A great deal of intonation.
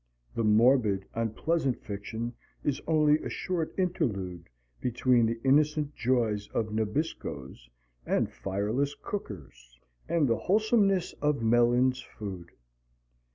Yes: wide, 6.0 semitones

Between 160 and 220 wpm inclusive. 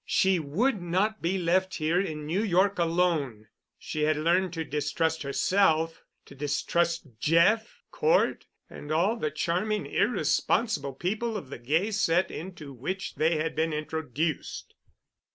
No: average, 140 wpm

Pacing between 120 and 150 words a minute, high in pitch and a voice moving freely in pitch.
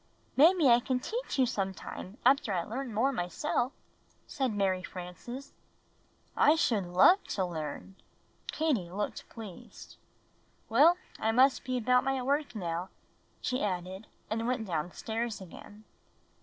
Yes: slow, 135 wpm; high, 225 Hz; wide, 5.9 semitones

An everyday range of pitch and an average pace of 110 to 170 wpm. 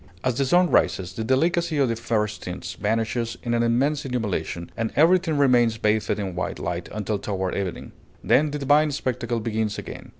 No: average, 4.7 semitones; average, 180 wpm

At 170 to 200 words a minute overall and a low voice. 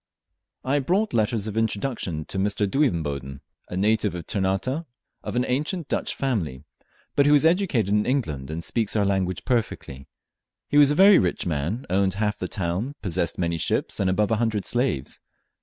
Yes: average, 175 wpm; low, 105 Hz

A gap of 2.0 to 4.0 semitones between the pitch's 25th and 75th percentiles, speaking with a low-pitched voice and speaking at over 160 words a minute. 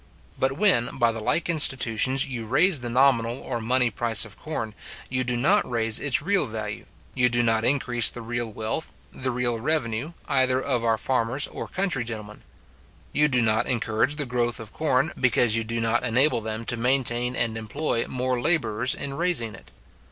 Yes: average, 2.9 semitones; low, 120 Hz; average, 185 wpm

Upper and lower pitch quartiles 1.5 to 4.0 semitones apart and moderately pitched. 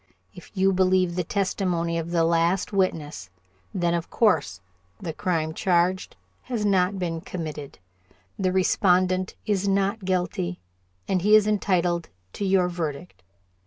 Yes: narrow, 2.4 semitones; medium, 180 Hz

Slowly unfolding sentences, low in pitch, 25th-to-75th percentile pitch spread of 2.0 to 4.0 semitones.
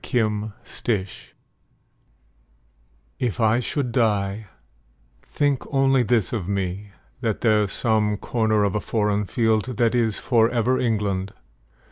Yes: slow, 120 wpm; low, 110 Hz; narrow, 2.6 semitones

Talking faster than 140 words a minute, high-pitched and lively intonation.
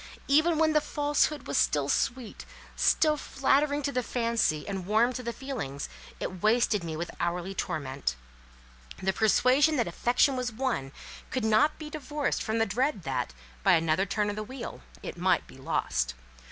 Yes: average, 170 wpm; high, 230 Hz; wide, 7.3 semitones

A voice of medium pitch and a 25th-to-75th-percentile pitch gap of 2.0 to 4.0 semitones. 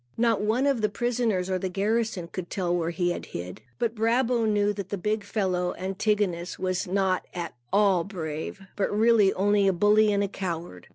No: high, 200 Hz; average, 3.1 semitones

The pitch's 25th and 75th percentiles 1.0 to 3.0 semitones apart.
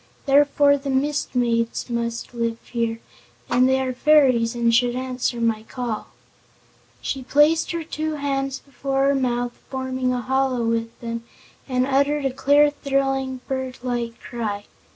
Yes: narrow, 2.6 semitones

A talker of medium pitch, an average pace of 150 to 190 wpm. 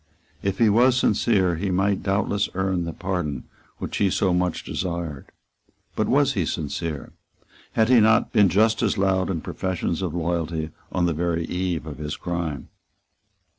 No: very low, 90 Hz; average, 165 wpm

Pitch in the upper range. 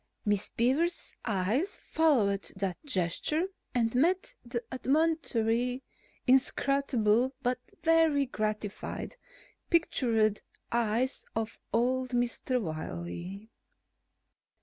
Yes: high, 245 Hz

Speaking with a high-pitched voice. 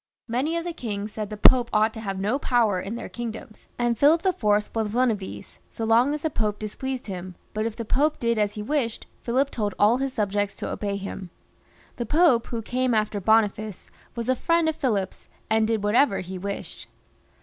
Yes: high, 225 Hz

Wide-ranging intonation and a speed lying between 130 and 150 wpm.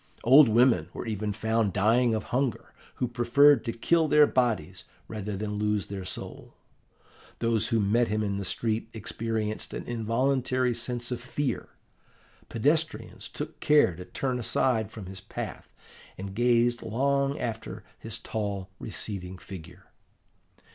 No: average, 3.2 semitones; average, 140 wpm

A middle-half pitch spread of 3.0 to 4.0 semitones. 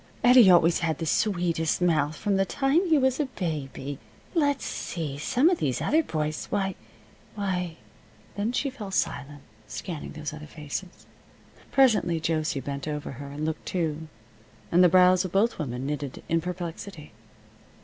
No: average, 5.0 semitones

